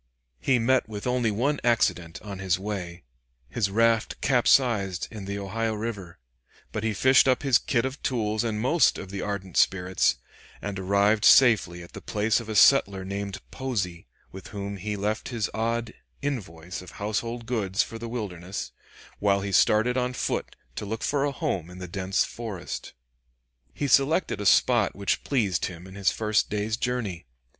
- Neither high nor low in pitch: No, low, 105 Hz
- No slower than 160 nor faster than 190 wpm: Yes, average, 175 wpm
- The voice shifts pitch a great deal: No, average, 3.5 semitones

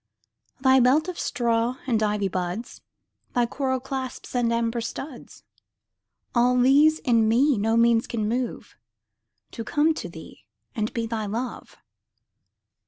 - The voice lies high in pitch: Yes, high, 240 Hz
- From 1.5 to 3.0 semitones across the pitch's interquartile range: Yes, narrow, 2.5 semitones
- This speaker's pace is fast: No, slow, 135 wpm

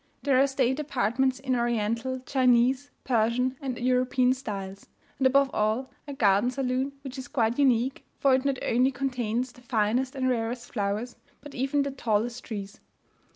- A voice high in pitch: Yes, very high, 255 Hz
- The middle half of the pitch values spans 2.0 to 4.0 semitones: Yes, narrow, 2.4 semitones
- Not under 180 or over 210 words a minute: No, average, 160 wpm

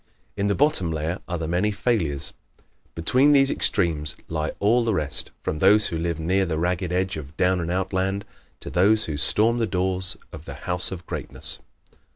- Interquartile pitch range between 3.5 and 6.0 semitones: Yes, average, 3.8 semitones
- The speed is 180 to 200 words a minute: Yes, average, 195 wpm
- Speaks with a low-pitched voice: Yes, very low, 90 Hz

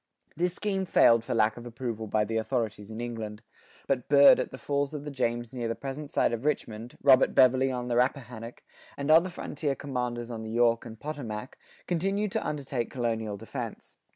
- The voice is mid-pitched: No, low, 125 Hz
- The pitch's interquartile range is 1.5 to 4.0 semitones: Yes, average, 3.6 semitones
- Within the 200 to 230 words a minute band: No, average, 190 wpm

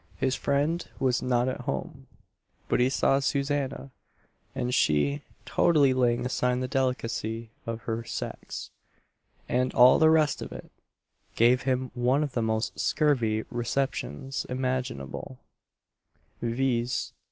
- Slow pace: Yes, slow, 125 wpm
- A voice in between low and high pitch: No, low, 125 Hz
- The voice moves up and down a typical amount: No, narrow, 2.3 semitones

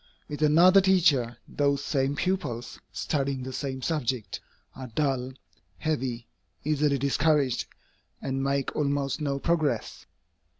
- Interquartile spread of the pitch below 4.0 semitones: Yes, narrow, 2.6 semitones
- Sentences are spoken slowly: Yes, slow, 115 wpm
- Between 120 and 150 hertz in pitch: Yes, medium, 140 Hz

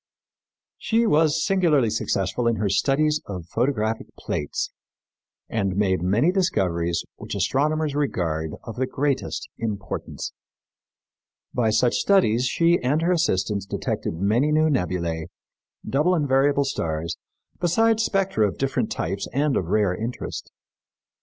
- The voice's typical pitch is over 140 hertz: No, low, 125 Hz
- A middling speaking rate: No, slow, 125 wpm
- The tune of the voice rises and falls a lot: Yes, wide, 7.8 semitones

